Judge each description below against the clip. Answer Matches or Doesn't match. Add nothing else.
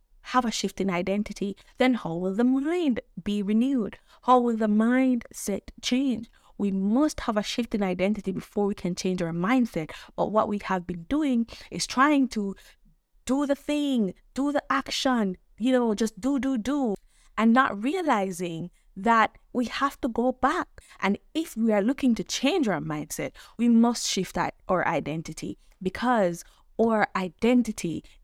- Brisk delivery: Doesn't match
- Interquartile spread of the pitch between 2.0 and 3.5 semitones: Doesn't match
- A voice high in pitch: Matches